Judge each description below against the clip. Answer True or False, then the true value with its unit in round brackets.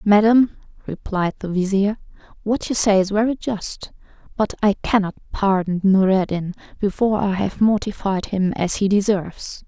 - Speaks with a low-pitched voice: False (200 Hz)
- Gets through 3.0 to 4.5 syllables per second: False (4.8 syllables/s)